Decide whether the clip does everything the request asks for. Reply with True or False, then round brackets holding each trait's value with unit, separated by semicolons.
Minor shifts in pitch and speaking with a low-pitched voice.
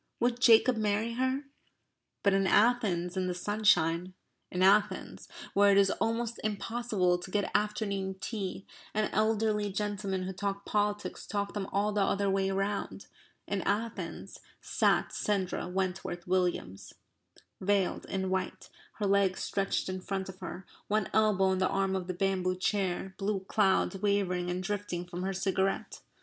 False (1.9 semitones; 195 Hz)